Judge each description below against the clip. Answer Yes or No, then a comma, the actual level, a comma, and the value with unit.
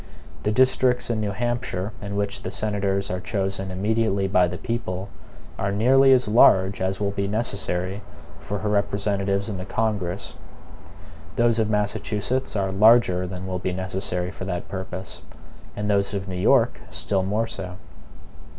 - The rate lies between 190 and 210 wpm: No, average, 160 wpm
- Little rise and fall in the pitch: Yes, narrow, 2.3 semitones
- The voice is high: No, low, 100 Hz